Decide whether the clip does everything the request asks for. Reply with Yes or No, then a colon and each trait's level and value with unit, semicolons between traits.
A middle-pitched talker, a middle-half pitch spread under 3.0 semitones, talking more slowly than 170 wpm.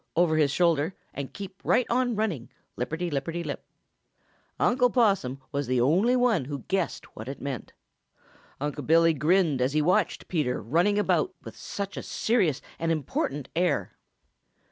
No: medium, 165 Hz; wide, 5.5 semitones; average, 160 wpm